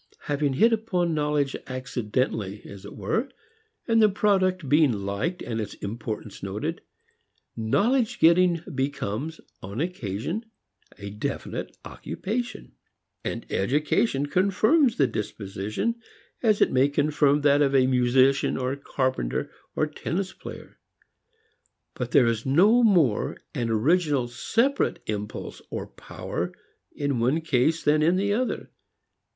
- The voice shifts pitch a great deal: Yes, wide, 7.8 semitones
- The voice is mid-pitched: Yes, medium, 145 Hz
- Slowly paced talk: Yes, slow, 125 wpm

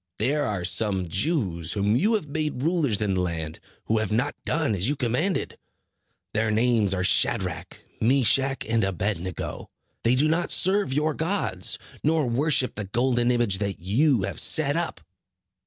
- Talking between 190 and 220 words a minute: No, average, 165 wpm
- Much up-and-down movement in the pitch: Yes, wide, 7.0 semitones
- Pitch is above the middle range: No, low, 120 Hz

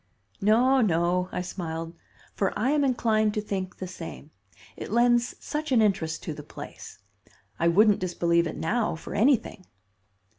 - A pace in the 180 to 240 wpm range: No, average, 155 wpm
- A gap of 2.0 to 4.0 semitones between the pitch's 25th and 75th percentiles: No, wide, 5.6 semitones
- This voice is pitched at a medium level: No, high, 195 Hz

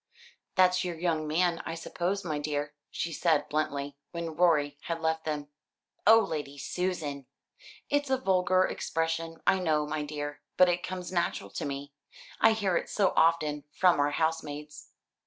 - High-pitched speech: No, medium, 165 Hz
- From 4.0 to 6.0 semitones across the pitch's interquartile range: No, average, 3.5 semitones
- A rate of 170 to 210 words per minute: No, average, 160 wpm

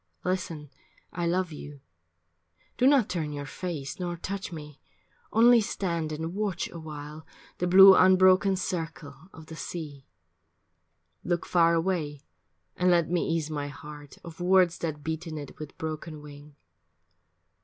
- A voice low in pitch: No, medium, 165 Hz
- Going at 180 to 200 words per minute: No, average, 145 wpm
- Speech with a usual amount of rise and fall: Yes, average, 3.3 semitones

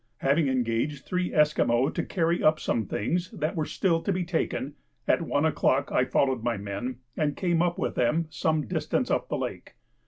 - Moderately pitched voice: Yes, medium, 150 Hz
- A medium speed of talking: Yes, average, 190 wpm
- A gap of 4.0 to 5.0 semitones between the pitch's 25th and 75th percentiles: Yes, average, 4.7 semitones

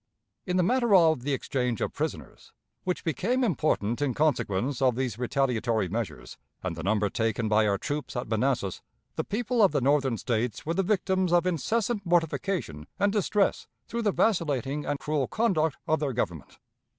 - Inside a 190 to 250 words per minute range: No, average, 175 wpm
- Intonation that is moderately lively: No, wide, 7.8 semitones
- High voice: No, medium, 145 Hz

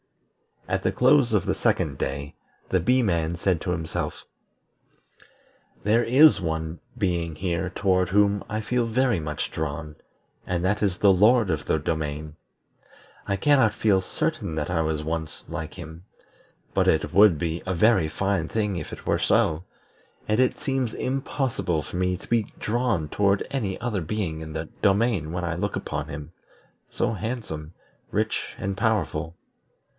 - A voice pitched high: No, very low, 90 Hz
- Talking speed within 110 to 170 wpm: Yes, average, 160 wpm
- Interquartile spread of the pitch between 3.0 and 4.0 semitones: No, average, 5.1 semitones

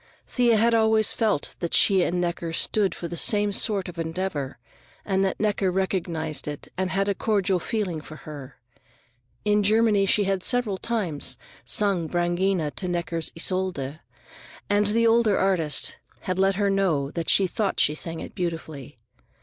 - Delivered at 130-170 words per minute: Yes, average, 165 wpm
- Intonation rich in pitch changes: No, average, 3.6 semitones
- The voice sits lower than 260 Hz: Yes, high, 190 Hz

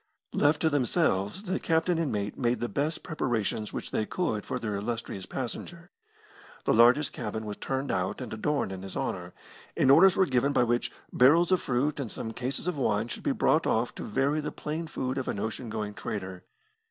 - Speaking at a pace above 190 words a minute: Yes, average, 200 wpm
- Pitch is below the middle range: Yes, low, 125 Hz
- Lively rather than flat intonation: Yes, wide, 5.9 semitones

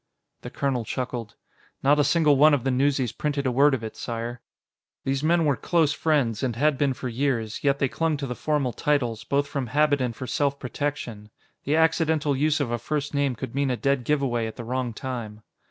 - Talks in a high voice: No, low, 135 Hz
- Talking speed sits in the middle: No, fast, 215 wpm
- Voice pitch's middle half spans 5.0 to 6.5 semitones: No, average, 3.1 semitones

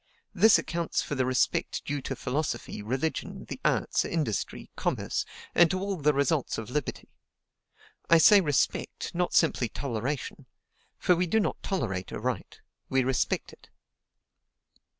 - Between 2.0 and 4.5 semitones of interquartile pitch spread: No, average, 5.0 semitones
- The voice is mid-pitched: Yes, medium, 150 Hz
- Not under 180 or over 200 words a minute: No, average, 145 wpm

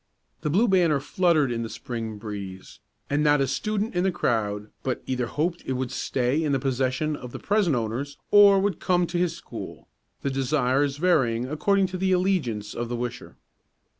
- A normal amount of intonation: No, wide, 6.4 semitones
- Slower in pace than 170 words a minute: No, average, 190 wpm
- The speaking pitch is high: No, medium, 140 Hz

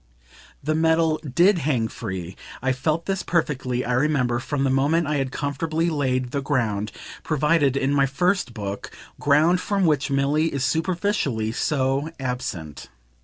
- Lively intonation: No, average, 4.0 semitones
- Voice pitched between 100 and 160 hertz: Yes, medium, 140 Hz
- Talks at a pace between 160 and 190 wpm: No, average, 150 wpm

